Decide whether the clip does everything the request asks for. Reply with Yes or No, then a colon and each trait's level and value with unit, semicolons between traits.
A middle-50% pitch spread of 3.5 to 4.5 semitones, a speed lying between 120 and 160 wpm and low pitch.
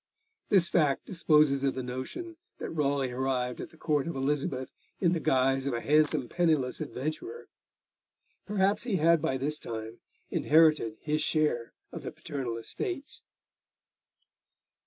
No: average, 4.1 semitones; average, 140 wpm; medium, 150 Hz